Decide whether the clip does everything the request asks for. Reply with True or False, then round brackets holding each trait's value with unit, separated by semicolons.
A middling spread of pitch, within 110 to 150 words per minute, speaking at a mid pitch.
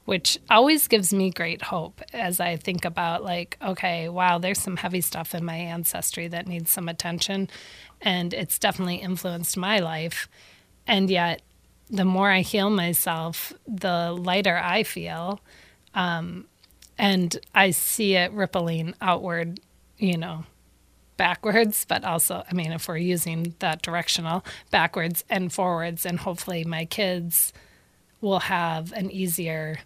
False (2.1 semitones; 145 wpm; 175 Hz)